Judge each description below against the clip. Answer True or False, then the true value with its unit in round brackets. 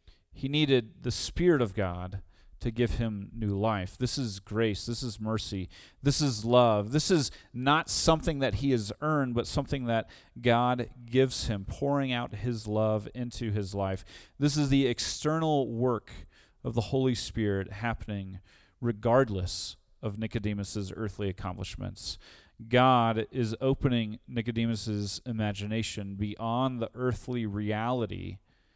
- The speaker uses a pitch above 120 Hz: False (115 Hz)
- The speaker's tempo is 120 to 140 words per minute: True (135 wpm)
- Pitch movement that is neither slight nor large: True (3.6 semitones)